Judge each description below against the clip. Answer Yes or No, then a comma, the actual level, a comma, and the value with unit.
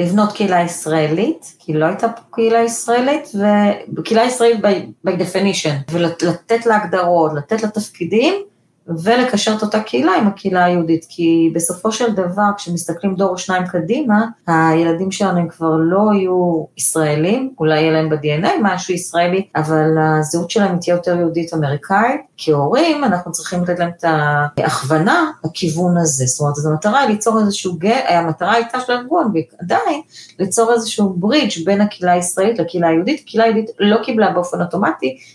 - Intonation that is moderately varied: Yes, average, 4.6 semitones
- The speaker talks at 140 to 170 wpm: Yes, average, 145 wpm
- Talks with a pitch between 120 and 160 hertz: No, medium, 180 Hz